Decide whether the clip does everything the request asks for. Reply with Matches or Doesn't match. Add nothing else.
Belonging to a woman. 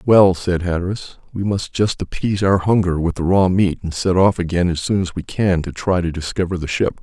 Doesn't match